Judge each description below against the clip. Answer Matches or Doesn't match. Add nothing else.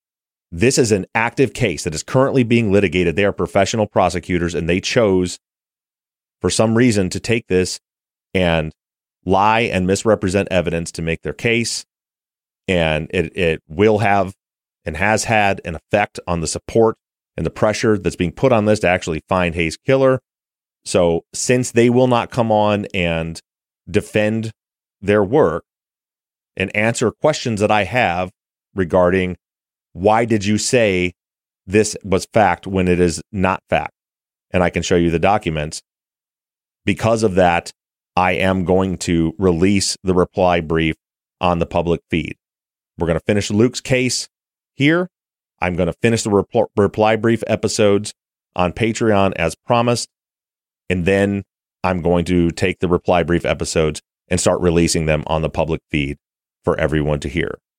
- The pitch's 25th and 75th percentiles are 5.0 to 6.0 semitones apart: Doesn't match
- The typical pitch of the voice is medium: Doesn't match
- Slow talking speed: Doesn't match